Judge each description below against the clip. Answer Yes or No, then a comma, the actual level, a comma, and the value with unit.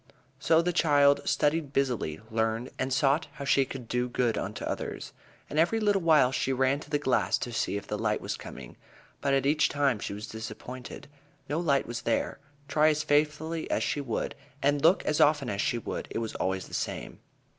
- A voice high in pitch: No, medium, 140 Hz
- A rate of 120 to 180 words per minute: No, fast, 205 wpm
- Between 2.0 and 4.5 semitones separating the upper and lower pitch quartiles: Yes, average, 4.0 semitones